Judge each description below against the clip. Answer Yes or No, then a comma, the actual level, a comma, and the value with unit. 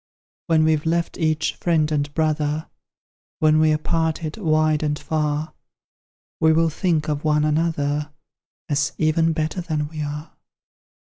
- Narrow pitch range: Yes, narrow, 1.2 semitones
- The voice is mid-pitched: Yes, medium, 155 Hz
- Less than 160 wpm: Yes, slow, 135 wpm